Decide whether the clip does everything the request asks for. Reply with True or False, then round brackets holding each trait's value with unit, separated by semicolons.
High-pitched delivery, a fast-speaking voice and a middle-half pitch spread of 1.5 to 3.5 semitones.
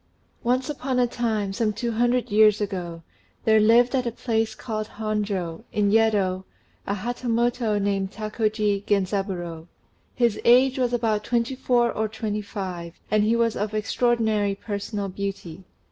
False (215 Hz; 145 wpm; 2.8 semitones)